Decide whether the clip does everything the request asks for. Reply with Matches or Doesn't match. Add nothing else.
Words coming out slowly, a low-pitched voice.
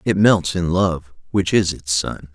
Doesn't match